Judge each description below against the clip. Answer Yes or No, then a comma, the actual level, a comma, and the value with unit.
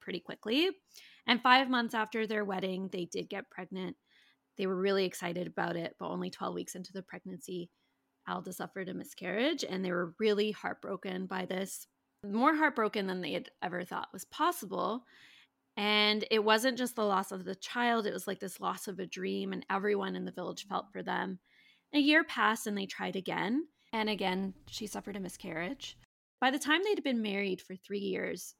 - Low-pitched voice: No, high, 200 Hz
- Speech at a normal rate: Yes, average, 195 wpm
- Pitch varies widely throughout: No, average, 3.5 semitones